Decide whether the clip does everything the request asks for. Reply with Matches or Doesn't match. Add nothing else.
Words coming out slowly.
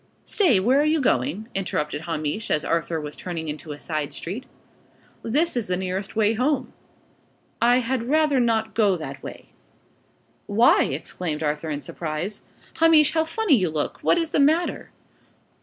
Doesn't match